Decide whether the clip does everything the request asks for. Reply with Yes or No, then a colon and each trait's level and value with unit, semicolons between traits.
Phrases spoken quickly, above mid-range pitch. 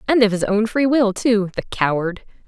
Yes: fast, 220 wpm; high, 215 Hz